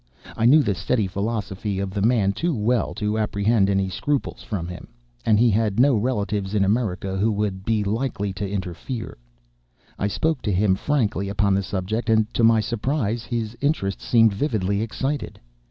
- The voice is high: No, low, 105 Hz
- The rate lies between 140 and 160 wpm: No, average, 175 wpm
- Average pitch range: Yes, average, 3.0 semitones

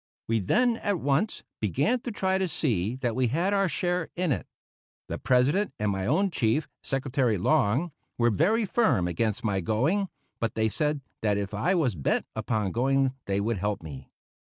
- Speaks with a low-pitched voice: Yes, low, 130 Hz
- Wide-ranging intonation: Yes, wide, 8.9 semitones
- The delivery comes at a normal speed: Yes, average, 180 wpm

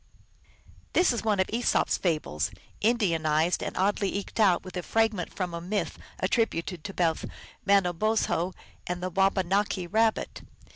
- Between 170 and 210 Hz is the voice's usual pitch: Yes, high, 190 Hz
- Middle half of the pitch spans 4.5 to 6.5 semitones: No, average, 3.5 semitones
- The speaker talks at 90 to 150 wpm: Yes, average, 145 wpm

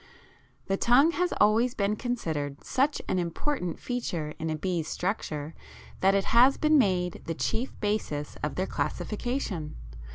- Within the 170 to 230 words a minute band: No, average, 150 wpm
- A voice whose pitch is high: Yes, high, 195 Hz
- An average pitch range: No, wide, 6.9 semitones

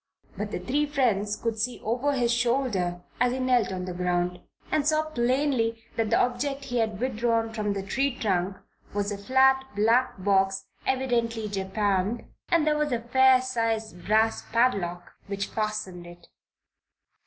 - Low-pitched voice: No, high, 225 Hz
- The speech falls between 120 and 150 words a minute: No, average, 160 wpm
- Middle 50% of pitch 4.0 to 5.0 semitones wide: Yes, average, 4.4 semitones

